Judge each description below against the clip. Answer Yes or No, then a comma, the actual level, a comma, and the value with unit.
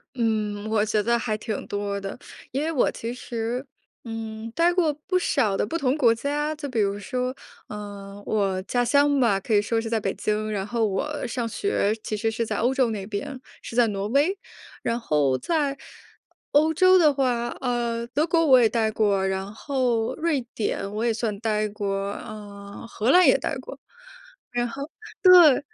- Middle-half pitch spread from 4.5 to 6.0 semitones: Yes, average, 4.8 semitones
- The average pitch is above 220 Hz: Yes, high, 230 Hz